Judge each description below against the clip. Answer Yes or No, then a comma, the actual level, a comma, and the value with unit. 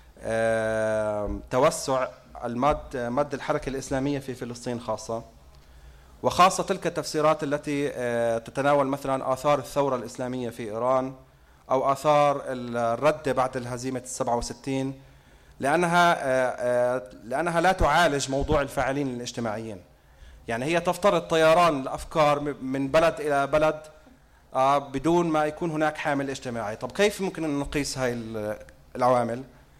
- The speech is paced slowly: Yes, slow, 120 wpm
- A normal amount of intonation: Yes, average, 3.7 semitones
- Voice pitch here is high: No, low, 135 Hz